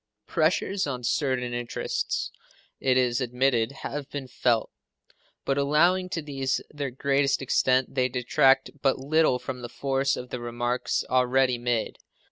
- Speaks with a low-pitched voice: Yes, low, 130 Hz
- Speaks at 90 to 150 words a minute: Yes, average, 140 wpm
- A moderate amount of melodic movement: No, narrow, 2.0 semitones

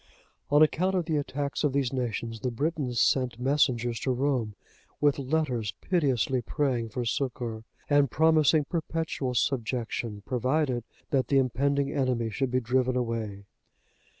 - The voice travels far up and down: No, average, 3.3 semitones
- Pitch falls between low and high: No, low, 130 Hz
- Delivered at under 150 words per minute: Yes, average, 140 wpm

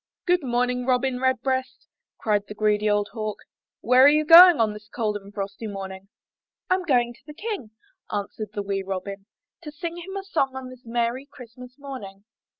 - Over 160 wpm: Yes, average, 180 wpm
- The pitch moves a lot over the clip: No, average, 4.6 semitones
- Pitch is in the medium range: No, high, 245 Hz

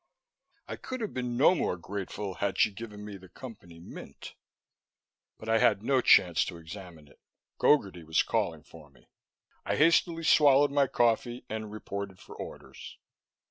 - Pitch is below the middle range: Yes, low, 105 Hz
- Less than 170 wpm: Yes, average, 160 wpm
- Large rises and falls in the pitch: Yes, wide, 5.9 semitones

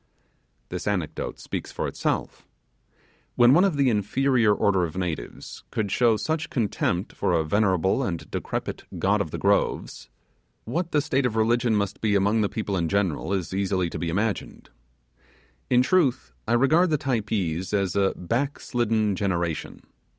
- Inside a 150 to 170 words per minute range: Yes, average, 160 wpm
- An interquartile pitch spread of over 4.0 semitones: Yes, average, 4.9 semitones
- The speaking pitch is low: Yes, low, 105 Hz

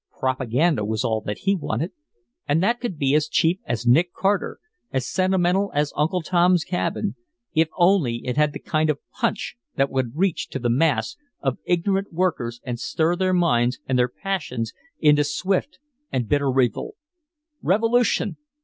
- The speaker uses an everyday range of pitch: No, wide, 6.3 semitones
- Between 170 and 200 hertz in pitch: No, medium, 150 Hz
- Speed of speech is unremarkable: Yes, average, 165 wpm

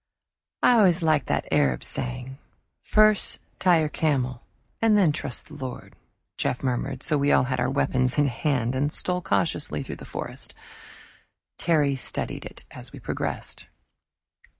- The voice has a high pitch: No, medium, 140 Hz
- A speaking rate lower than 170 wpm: Yes, average, 155 wpm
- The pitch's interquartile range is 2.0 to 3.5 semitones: No, average, 4.2 semitones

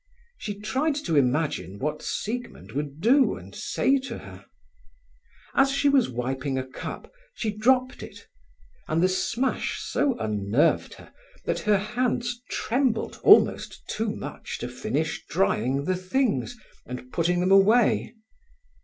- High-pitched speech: Yes, high, 205 Hz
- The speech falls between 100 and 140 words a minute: Yes, slow, 135 wpm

